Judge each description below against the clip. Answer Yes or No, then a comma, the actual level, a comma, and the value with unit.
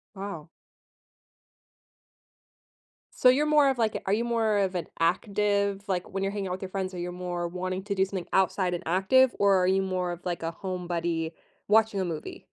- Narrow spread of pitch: Yes, narrow, 2.3 semitones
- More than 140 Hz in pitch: Yes, high, 190 Hz